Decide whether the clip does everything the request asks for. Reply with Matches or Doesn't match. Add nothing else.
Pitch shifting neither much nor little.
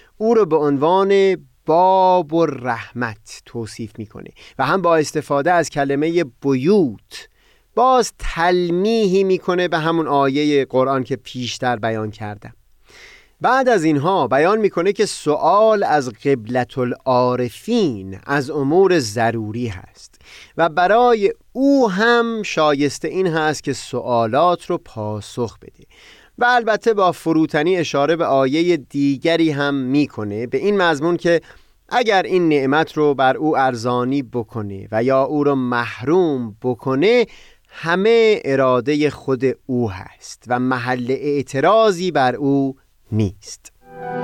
Doesn't match